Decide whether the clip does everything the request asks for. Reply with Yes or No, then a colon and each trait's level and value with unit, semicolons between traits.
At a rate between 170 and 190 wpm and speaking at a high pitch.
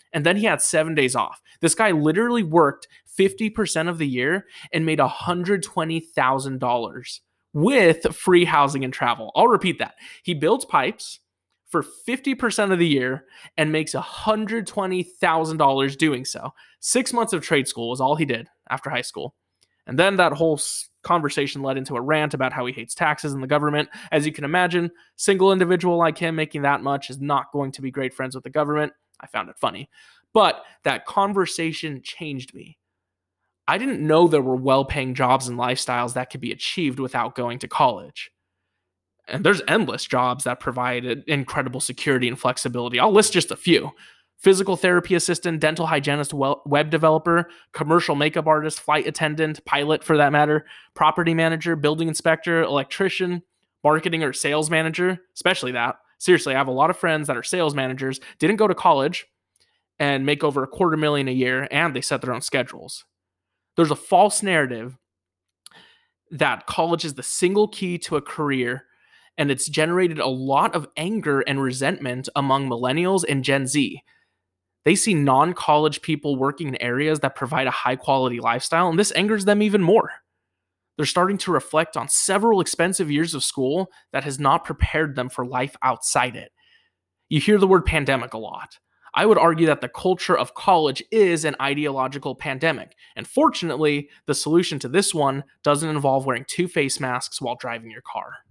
No: average, 175 wpm; medium, 150 Hz